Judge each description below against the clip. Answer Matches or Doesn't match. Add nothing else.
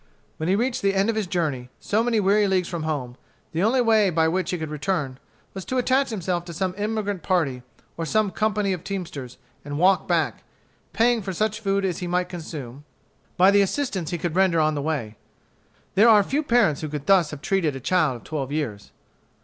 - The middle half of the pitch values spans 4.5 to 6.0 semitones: Matches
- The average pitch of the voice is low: Doesn't match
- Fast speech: Matches